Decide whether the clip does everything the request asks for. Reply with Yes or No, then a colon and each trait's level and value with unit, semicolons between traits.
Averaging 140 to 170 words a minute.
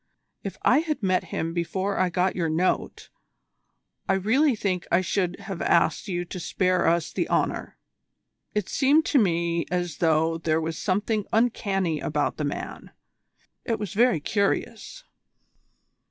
Yes: average, 150 wpm